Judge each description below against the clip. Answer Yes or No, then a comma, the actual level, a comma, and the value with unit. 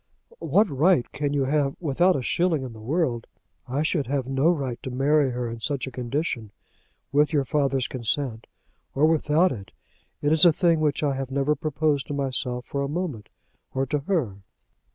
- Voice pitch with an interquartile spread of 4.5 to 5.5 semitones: No, average, 3.1 semitones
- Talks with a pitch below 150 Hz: Yes, medium, 140 Hz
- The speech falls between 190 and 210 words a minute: Yes, average, 195 wpm